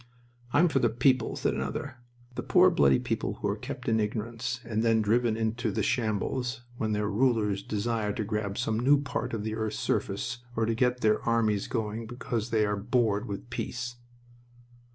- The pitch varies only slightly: Yes, narrow, 2.3 semitones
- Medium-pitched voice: No, low, 115 Hz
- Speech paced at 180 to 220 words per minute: Yes, average, 185 wpm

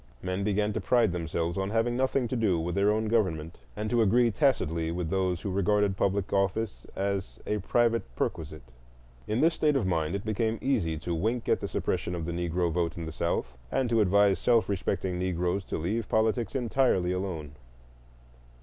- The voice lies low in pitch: Yes, low, 100 Hz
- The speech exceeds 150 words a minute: Yes, average, 190 wpm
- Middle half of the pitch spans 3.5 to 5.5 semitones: Yes, average, 4.5 semitones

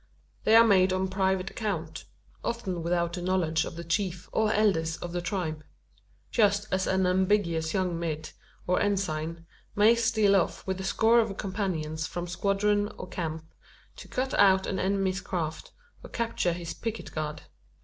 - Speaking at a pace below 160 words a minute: No, average, 165 wpm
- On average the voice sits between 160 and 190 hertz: Yes, medium, 185 Hz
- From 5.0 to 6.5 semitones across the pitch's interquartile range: No, average, 3.3 semitones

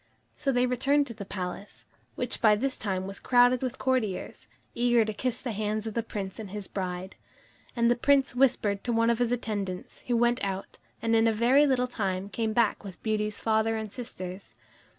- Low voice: No, high, 225 Hz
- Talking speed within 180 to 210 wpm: Yes, average, 200 wpm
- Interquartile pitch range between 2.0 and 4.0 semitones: Yes, average, 3.3 semitones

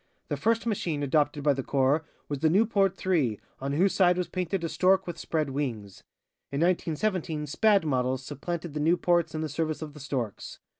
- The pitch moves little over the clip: No, average, 4.2 semitones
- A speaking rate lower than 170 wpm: No, average, 190 wpm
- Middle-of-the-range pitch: Yes, medium, 155 Hz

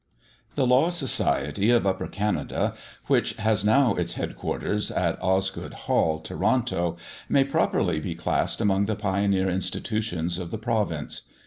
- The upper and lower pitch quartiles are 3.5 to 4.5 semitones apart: Yes, average, 4.2 semitones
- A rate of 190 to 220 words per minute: No, slow, 135 wpm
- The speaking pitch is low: Yes, low, 100 Hz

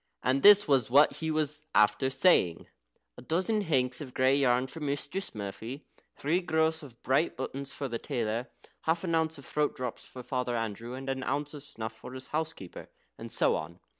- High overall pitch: No, low, 135 Hz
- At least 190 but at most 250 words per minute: Yes, average, 195 wpm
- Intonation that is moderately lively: Yes, average, 4.1 semitones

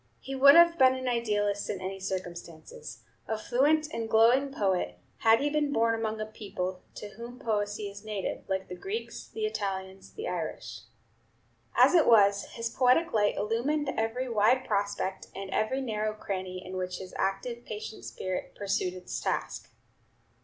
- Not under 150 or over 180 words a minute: Yes, average, 165 wpm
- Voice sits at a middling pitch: No, high, 215 Hz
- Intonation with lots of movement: No, average, 4.5 semitones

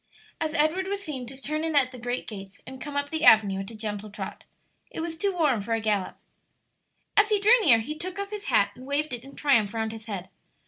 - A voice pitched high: Yes, very high, 265 Hz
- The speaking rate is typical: No, fast, 245 wpm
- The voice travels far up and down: Yes, wide, 6.5 semitones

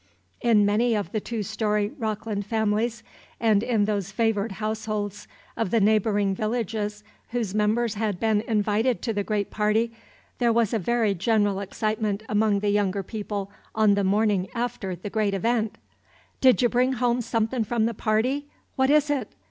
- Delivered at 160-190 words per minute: Yes, average, 165 wpm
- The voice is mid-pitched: No, high, 215 Hz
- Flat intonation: Yes, narrow, 2.0 semitones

